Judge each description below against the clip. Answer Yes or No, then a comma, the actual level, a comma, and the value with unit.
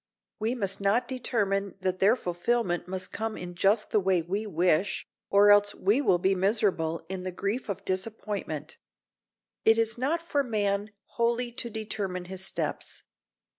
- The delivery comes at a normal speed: Yes, average, 160 wpm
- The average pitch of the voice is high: Yes, high, 200 Hz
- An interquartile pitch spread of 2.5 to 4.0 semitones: Yes, average, 3.3 semitones